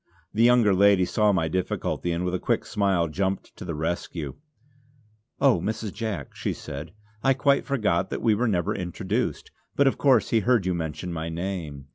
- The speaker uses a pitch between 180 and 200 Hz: No, very low, 95 Hz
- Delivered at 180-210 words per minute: Yes, average, 185 wpm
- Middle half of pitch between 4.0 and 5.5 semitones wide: Yes, average, 4.6 semitones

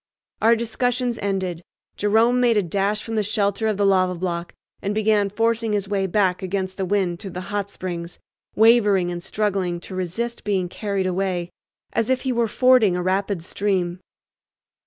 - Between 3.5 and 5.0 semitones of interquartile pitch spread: No, average, 3.0 semitones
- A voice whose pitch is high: Yes, high, 200 Hz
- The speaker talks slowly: No, average, 175 wpm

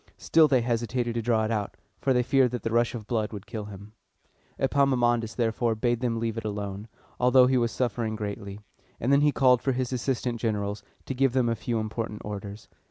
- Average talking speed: No, fast, 210 wpm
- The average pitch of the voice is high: No, low, 115 Hz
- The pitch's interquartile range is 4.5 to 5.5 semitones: No, narrow, 2.6 semitones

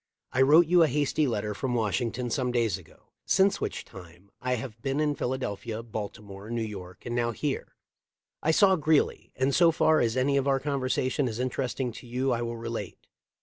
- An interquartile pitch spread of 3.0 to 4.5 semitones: Yes, average, 3.7 semitones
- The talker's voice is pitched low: Yes, low, 125 Hz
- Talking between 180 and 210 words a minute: Yes, average, 190 wpm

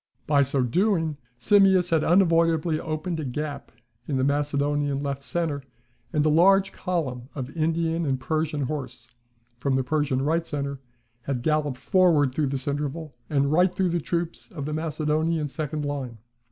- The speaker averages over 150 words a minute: Yes, average, 160 wpm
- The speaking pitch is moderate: Yes, medium, 150 Hz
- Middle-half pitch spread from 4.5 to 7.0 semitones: No, average, 2.9 semitones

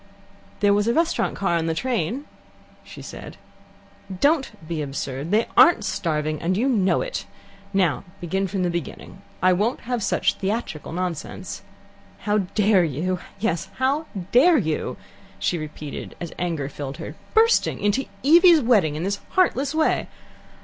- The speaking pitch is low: No, high, 195 Hz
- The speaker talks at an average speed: Yes, average, 155 wpm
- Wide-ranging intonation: Yes, wide, 7.2 semitones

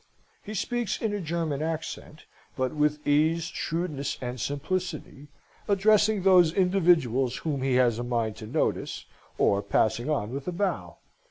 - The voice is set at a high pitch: No, medium, 155 Hz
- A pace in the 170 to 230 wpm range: No, average, 150 wpm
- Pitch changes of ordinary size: No, wide, 5.7 semitones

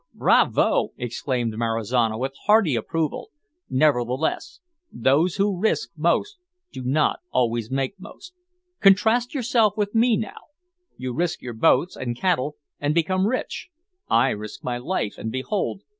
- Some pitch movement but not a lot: No, wide, 8.3 semitones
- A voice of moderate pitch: Yes, medium, 150 Hz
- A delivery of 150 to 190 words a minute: No, slow, 135 wpm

